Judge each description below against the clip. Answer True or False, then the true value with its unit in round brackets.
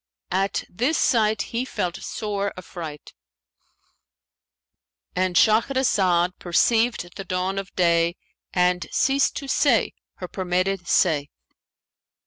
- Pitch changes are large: False (3.8 semitones)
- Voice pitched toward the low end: False (185 Hz)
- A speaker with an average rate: False (100 wpm)